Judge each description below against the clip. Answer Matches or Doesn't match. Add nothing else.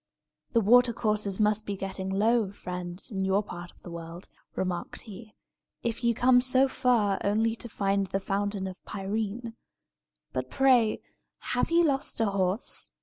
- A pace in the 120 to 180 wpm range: Matches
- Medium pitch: Doesn't match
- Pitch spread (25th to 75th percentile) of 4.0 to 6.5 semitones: Doesn't match